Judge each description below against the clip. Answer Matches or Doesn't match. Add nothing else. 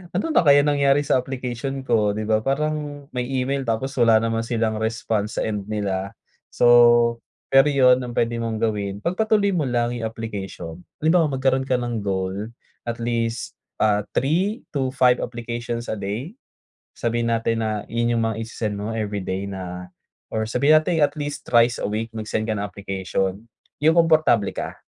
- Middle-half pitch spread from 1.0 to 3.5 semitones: Doesn't match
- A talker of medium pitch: Doesn't match